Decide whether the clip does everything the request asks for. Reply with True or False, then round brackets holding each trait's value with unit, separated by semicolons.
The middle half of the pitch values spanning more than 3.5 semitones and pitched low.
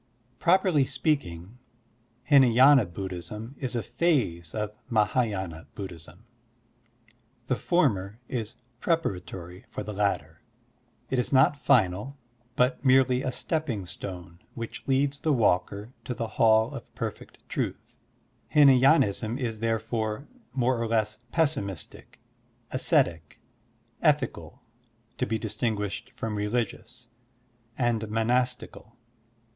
True (4.4 semitones; 115 Hz)